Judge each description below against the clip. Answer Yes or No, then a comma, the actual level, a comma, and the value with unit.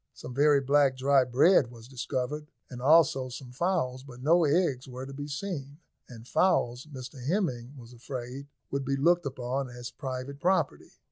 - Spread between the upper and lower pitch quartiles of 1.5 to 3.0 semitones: Yes, narrow, 2.6 semitones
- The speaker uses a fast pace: No, average, 165 wpm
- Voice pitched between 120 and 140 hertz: Yes, low, 135 Hz